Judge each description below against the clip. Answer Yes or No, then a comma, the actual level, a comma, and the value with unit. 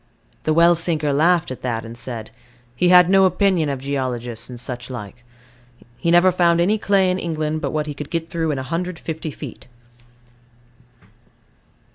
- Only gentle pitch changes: No, average, 5.1 semitones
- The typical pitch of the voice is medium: Yes, medium, 155 Hz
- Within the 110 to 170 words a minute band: Yes, average, 165 wpm